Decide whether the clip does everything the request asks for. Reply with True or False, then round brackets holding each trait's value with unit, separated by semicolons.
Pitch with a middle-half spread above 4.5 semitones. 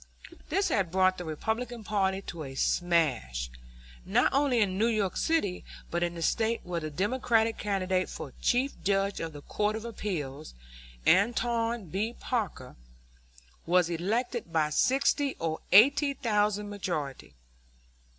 True (5.2 semitones)